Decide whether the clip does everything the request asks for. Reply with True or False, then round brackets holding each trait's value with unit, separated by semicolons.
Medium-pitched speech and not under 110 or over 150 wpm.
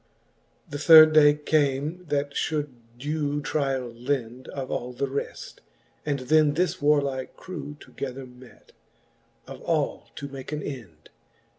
True (145 Hz; 140 wpm)